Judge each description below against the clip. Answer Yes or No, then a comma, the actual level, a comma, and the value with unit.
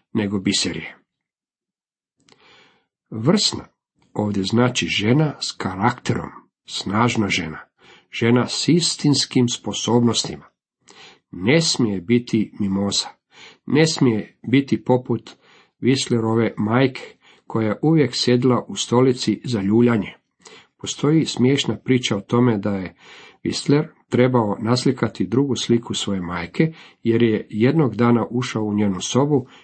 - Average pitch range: Yes, average, 3.4 semitones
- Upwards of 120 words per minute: No, slow, 110 wpm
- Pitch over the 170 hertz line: No, low, 120 Hz